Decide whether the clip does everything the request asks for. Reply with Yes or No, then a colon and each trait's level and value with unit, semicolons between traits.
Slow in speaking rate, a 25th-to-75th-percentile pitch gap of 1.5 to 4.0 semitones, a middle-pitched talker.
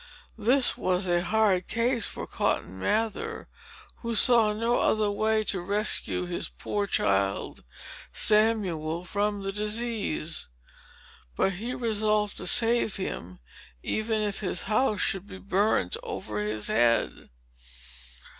No: slow, 125 wpm; average, 3.6 semitones; high, 210 Hz